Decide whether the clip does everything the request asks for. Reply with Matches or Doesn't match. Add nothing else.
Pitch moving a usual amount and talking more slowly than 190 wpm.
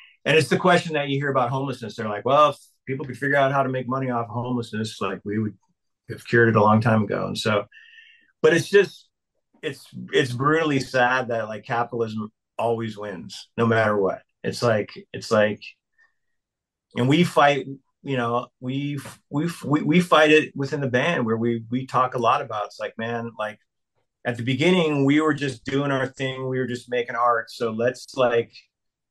Doesn't match